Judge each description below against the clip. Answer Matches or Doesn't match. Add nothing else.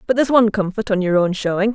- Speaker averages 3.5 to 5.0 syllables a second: Doesn't match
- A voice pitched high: Matches